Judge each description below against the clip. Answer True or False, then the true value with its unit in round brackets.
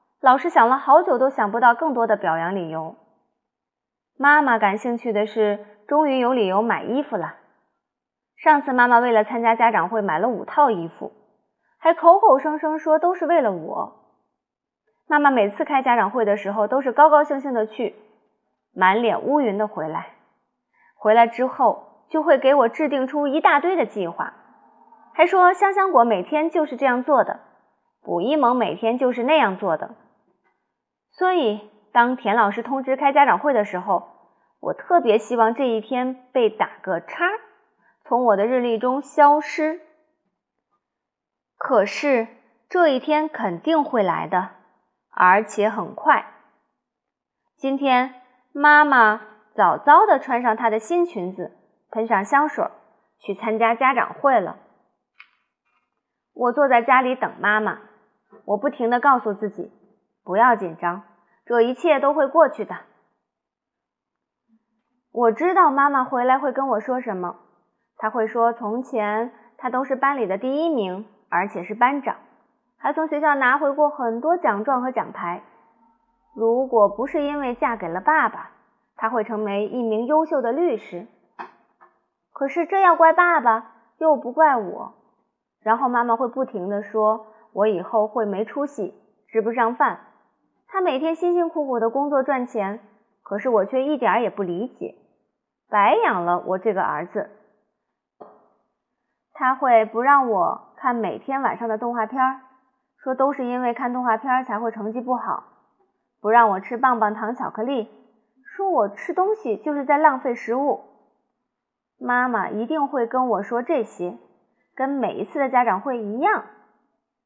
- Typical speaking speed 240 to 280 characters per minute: False (220 characters per minute)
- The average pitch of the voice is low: False (245 Hz)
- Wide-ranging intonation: False (4.8 semitones)